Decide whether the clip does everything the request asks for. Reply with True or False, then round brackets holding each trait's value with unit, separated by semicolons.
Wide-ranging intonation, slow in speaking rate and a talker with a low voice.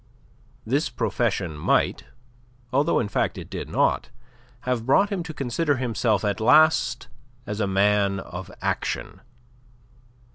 True (6.0 semitones; 130 wpm; 110 Hz)